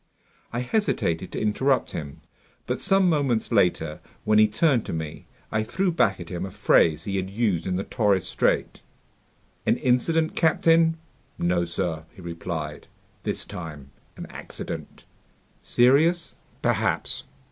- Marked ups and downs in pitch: Yes, wide, 8.2 semitones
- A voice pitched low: Yes, low, 105 Hz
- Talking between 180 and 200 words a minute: No, average, 140 wpm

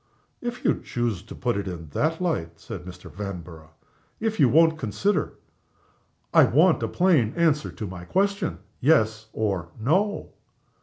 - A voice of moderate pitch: No, low, 120 Hz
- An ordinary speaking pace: Yes, average, 155 wpm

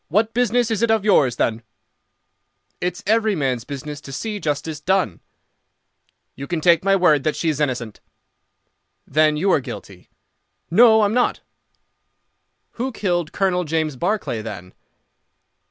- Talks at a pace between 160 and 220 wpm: No, average, 145 wpm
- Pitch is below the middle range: No, medium, 170 Hz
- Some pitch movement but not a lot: No, wide, 6.5 semitones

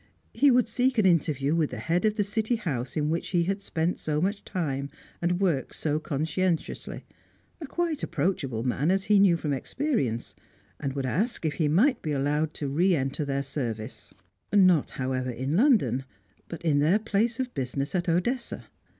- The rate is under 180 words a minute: No, average, 185 wpm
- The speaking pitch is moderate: Yes, medium, 165 Hz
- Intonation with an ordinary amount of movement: No, wide, 6.3 semitones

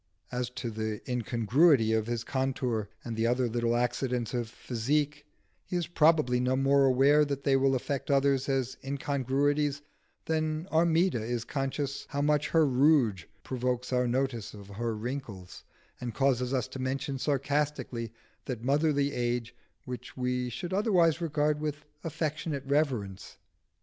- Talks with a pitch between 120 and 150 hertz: Yes, low, 135 Hz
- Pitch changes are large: No, average, 3.4 semitones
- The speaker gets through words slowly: No, average, 145 wpm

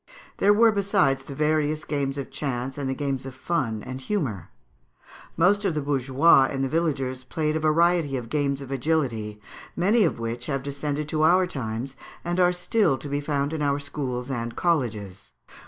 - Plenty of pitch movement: No, average, 3.5 semitones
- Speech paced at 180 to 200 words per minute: Yes, average, 185 wpm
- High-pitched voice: No, medium, 140 Hz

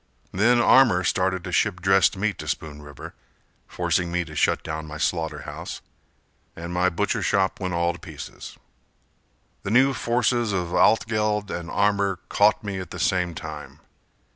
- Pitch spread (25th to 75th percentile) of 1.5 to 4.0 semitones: Yes, average, 3.6 semitones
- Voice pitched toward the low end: Yes, very low, 90 Hz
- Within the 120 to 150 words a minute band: No, average, 165 wpm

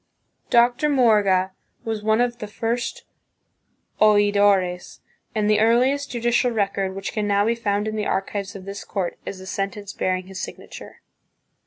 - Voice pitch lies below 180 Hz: No, high, 210 Hz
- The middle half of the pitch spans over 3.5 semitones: No, average, 2.8 semitones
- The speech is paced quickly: No, average, 155 wpm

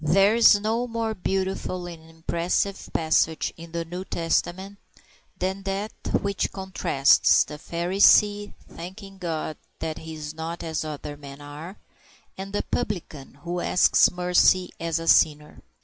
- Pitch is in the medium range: Yes, medium, 175 Hz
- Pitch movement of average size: Yes, average, 3.4 semitones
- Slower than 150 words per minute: Yes, average, 140 wpm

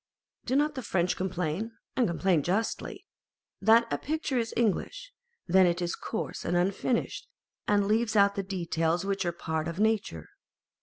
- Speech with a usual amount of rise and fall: Yes, average, 4.6 semitones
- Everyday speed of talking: Yes, average, 165 wpm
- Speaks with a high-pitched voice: Yes, high, 195 Hz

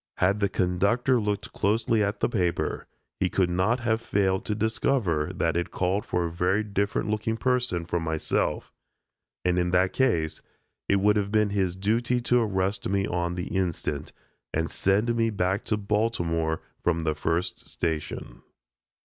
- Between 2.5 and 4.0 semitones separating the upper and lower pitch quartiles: Yes, average, 3.6 semitones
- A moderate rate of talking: Yes, average, 165 wpm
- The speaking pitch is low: Yes, very low, 95 Hz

